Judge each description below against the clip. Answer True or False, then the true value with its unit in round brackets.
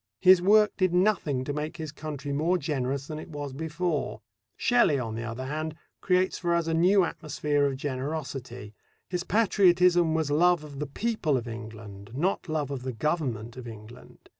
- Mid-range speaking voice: True (150 Hz)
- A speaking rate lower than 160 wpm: False (180 wpm)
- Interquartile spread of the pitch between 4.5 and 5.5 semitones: True (5.0 semitones)